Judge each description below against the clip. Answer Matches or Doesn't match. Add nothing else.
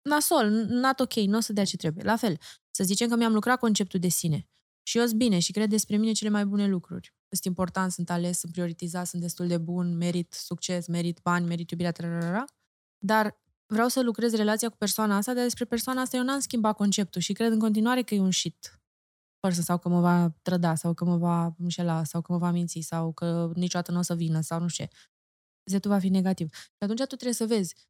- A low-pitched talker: Doesn't match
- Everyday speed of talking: Doesn't match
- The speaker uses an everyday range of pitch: Matches